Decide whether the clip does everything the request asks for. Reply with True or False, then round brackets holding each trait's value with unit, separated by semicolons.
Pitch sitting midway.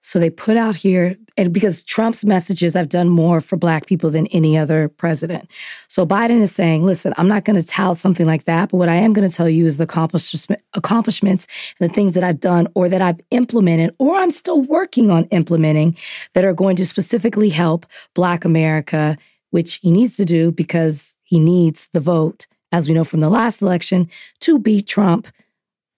True (180 Hz)